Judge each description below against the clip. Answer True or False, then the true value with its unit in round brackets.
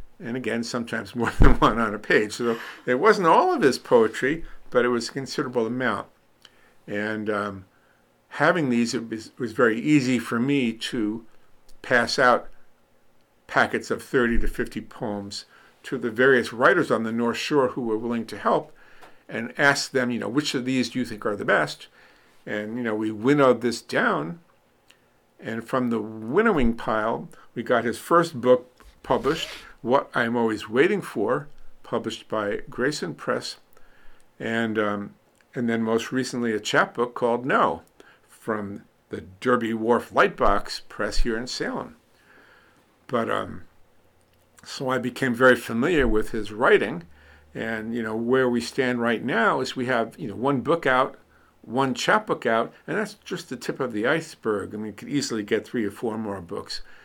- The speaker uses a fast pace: False (170 wpm)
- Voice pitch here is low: True (115 Hz)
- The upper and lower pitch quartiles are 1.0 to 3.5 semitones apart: True (2.7 semitones)